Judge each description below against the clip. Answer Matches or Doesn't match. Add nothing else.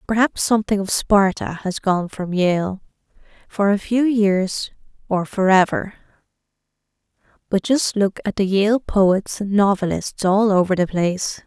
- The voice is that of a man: Doesn't match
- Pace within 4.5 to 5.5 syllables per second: Doesn't match